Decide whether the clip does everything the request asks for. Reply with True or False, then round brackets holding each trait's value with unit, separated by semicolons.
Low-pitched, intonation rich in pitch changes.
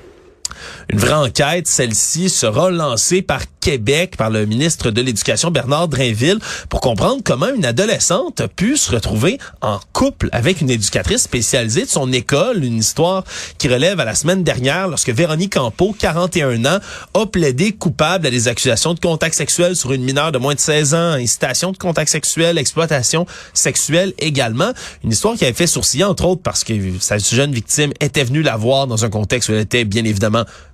False (145 Hz; 6.2 semitones)